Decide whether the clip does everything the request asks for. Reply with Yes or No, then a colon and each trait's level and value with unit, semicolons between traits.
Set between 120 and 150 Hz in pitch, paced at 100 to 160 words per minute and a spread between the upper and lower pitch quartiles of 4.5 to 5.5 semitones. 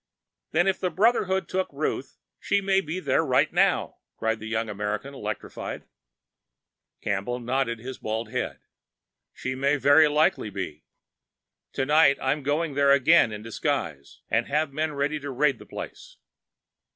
Yes: medium, 140 Hz; average, 150 wpm; average, 5.2 semitones